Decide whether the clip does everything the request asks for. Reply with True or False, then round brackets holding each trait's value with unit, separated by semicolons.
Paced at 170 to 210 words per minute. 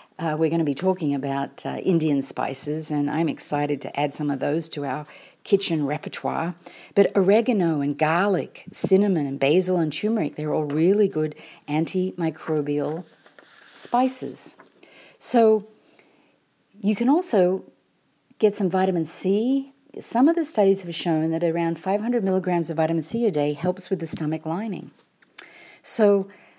False (150 wpm)